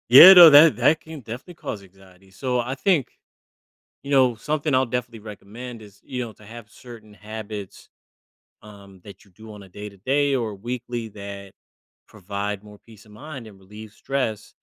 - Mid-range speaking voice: No, low, 110 Hz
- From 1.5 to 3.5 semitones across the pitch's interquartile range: No, average, 4.0 semitones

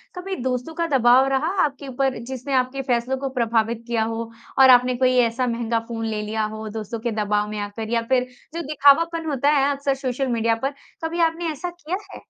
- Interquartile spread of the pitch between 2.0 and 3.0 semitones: No, average, 3.5 semitones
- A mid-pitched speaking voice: No, very high, 255 Hz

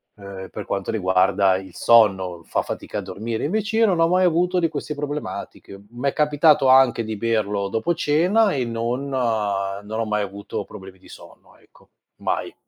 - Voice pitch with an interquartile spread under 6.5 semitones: No, wide, 7.1 semitones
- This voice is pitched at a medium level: No, low, 115 Hz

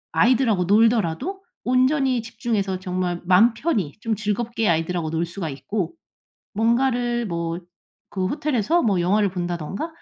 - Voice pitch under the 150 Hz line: No, high, 210 Hz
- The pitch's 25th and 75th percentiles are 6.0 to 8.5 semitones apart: No, average, 5.1 semitones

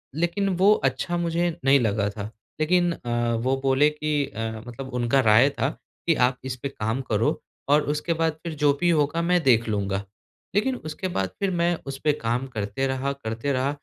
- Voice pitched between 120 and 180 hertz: Yes, low, 135 Hz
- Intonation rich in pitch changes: Yes, wide, 5.8 semitones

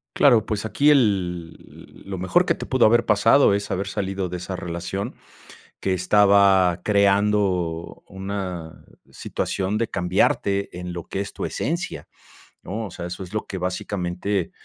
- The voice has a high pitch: No, low, 100 Hz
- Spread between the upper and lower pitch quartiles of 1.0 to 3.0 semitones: Yes, narrow, 2.6 semitones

